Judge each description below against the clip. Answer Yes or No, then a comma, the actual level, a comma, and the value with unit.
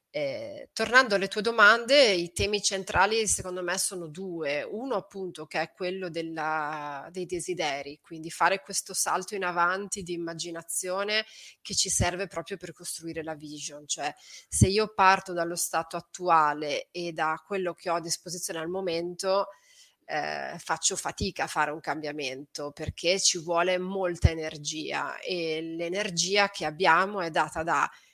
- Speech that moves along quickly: No, average, 150 wpm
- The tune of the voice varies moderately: Yes, average, 3.1 semitones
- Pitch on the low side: No, medium, 175 Hz